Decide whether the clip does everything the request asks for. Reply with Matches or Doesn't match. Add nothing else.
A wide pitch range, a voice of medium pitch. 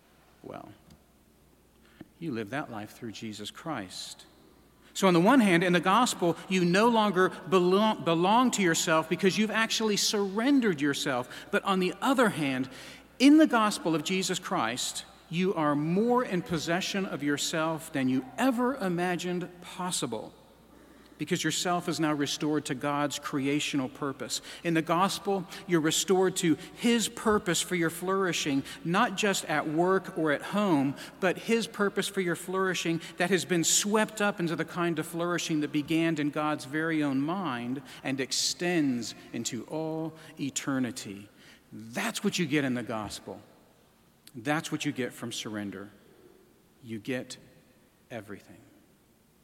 Doesn't match